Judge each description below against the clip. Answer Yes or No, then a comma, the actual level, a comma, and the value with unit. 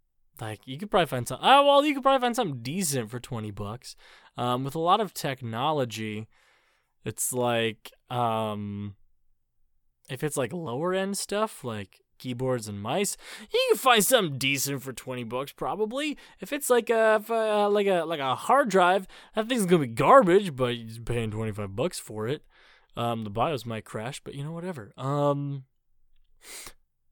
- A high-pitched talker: No, low, 135 Hz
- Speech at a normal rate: Yes, average, 180 wpm